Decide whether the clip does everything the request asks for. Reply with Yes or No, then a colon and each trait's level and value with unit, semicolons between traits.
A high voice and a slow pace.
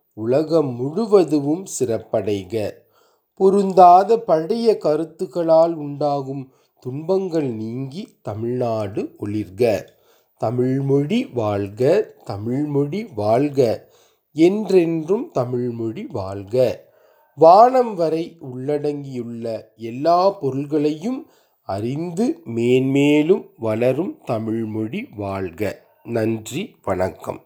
No: medium, 145 Hz; slow, 65 wpm